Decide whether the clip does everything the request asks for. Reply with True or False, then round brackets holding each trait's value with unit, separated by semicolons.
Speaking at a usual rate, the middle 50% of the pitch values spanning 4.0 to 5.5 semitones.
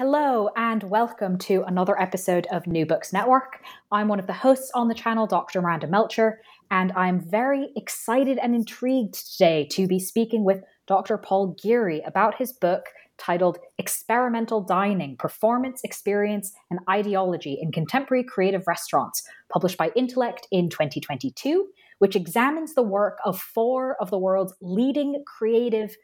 True (150 wpm; 4.4 semitones)